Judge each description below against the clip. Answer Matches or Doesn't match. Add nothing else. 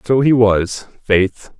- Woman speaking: Doesn't match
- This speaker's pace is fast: Doesn't match